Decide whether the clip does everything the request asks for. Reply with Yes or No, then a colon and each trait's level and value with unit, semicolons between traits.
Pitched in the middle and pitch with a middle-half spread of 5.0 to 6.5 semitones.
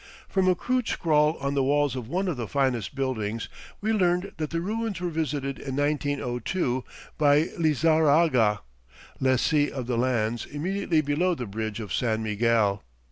Yes: medium, 145 Hz; average, 5.3 semitones